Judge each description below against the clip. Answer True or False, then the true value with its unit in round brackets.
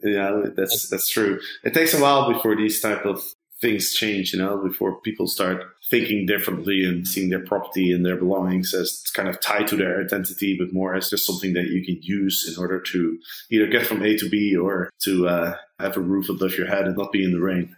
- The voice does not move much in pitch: True (1.8 semitones)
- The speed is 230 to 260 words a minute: True (235 wpm)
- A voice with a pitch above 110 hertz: False (95 Hz)